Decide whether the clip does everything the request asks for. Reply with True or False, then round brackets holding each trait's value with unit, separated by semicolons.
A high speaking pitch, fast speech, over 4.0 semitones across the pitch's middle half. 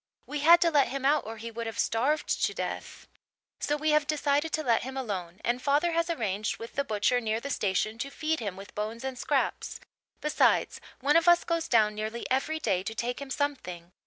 True (260 Hz; 220 wpm; 5.3 semitones)